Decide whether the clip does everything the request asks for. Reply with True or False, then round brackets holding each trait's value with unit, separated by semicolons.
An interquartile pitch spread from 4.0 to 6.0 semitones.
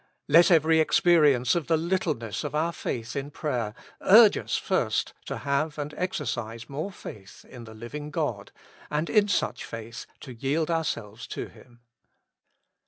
True (5.5 semitones)